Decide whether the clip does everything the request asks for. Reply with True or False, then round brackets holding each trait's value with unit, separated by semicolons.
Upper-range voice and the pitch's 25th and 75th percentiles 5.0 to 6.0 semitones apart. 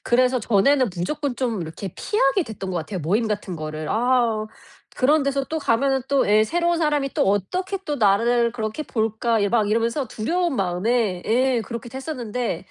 False (235 Hz; 4.5 semitones)